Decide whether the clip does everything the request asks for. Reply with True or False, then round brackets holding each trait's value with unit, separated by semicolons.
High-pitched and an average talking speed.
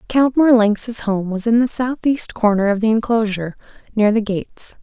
True (225 Hz; 175 wpm)